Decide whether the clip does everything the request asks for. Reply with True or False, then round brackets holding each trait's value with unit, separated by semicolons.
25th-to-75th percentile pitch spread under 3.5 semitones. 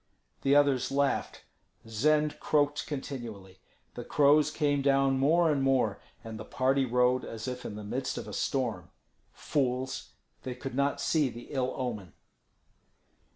True (2.5 semitones)